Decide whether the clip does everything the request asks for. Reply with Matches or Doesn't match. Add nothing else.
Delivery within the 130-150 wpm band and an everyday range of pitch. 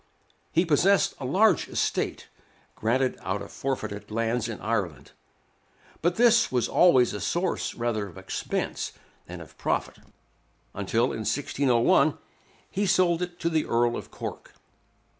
Doesn't match